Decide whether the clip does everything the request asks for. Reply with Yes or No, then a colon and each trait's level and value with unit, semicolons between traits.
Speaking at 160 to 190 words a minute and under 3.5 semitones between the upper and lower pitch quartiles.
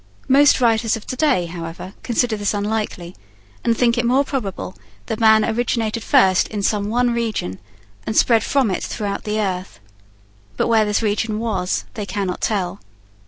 Yes: average, 165 wpm; average, 2.8 semitones